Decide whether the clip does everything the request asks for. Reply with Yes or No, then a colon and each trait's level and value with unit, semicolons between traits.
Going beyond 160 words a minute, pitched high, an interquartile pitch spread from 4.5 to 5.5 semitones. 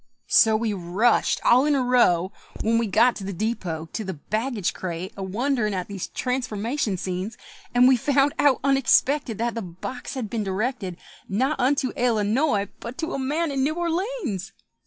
Yes: average, 180 wpm; high, 235 Hz; average, 5.2 semitones